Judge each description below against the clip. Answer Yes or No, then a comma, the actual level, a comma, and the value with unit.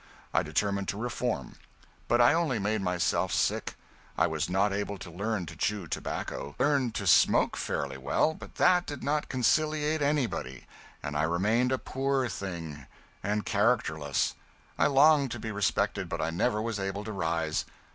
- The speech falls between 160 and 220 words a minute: Yes, average, 170 wpm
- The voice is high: No, low, 105 Hz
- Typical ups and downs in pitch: No, wide, 6.8 semitones